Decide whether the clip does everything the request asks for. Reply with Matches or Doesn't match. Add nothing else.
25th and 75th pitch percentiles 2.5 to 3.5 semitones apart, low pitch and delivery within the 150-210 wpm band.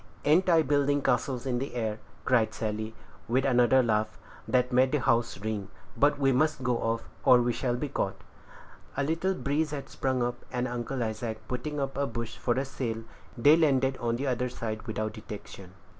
Matches